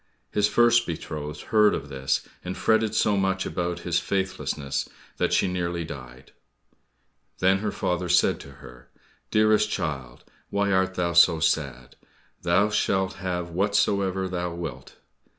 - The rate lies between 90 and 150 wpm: Yes, average, 140 wpm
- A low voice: Yes, very low, 90 Hz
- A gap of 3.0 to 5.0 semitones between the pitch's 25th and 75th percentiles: Yes, average, 3.7 semitones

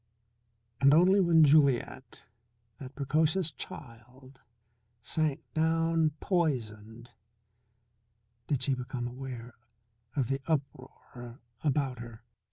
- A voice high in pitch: No, low, 135 Hz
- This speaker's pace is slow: Yes, slow, 90 wpm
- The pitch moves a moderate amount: Yes, average, 4.4 semitones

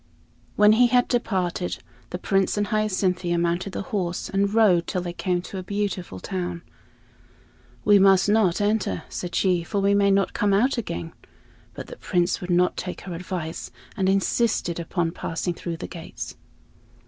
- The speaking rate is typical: Yes, average, 170 wpm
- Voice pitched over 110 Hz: Yes, medium, 185 Hz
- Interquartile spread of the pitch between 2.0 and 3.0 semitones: Yes, narrow, 2.6 semitones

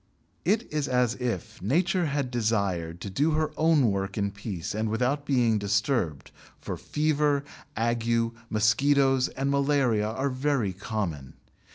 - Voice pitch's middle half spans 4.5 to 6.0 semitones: Yes, average, 5.2 semitones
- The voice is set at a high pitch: No, low, 120 Hz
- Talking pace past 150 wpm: No, average, 140 wpm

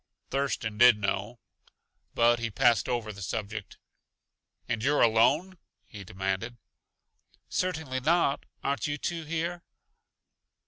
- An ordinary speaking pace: No, slow, 110 wpm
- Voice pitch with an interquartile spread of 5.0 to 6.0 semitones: Yes, wide, 5.4 semitones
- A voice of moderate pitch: No, low, 120 Hz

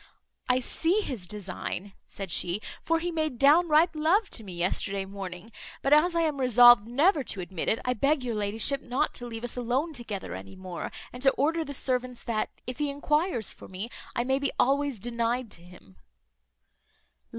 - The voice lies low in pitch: No, high, 245 Hz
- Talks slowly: No, average, 185 wpm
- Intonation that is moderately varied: No, wide, 6.3 semitones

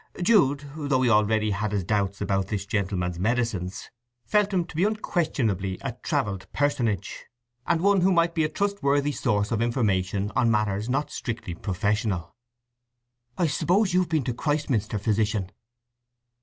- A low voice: Yes, low, 115 Hz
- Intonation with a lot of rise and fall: Yes, wide, 7.2 semitones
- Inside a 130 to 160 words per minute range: Yes, average, 150 wpm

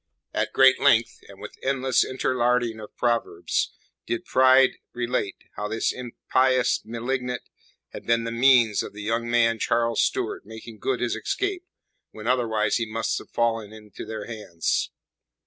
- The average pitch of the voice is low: Yes, low, 120 Hz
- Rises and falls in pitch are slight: Yes, narrow, 2.3 semitones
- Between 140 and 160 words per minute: Yes, average, 150 wpm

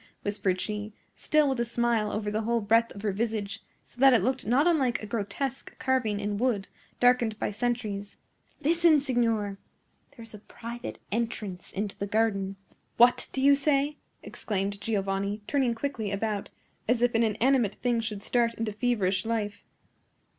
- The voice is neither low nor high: No, high, 225 Hz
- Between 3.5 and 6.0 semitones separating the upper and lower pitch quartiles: No, average, 3.1 semitones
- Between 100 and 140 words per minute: No, average, 165 wpm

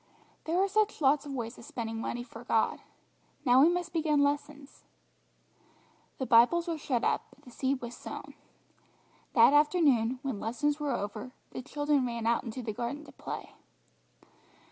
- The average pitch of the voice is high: Yes, very high, 270 Hz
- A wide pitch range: No, average, 4.0 semitones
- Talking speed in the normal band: Yes, average, 165 wpm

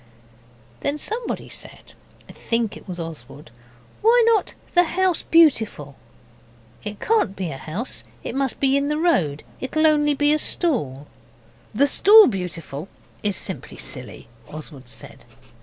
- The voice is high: Yes, very high, 260 Hz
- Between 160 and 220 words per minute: No, average, 140 wpm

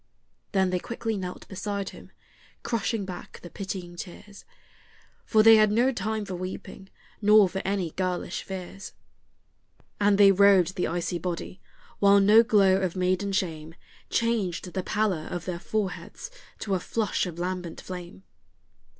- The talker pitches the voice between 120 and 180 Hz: No, high, 190 Hz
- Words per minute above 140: Yes, average, 150 wpm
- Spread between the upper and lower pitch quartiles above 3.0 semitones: No, narrow, 2.4 semitones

